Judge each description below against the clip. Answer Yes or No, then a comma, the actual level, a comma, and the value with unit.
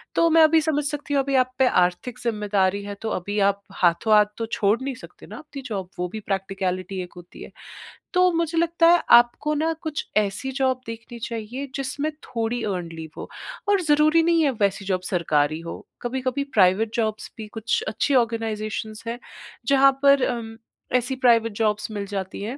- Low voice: No, high, 225 Hz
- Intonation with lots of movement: Yes, wide, 5.7 semitones